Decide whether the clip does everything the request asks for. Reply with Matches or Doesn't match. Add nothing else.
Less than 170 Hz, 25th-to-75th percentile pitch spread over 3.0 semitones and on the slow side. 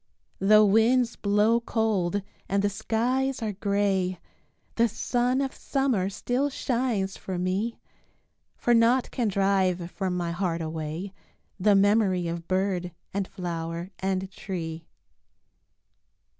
Doesn't match